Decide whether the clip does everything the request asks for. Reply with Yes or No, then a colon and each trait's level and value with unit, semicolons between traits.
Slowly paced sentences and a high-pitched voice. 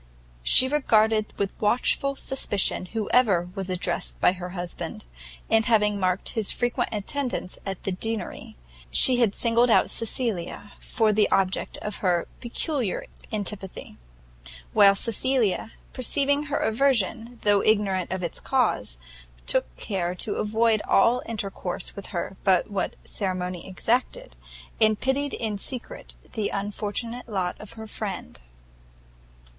Yes: slow, 130 wpm; high, 210 Hz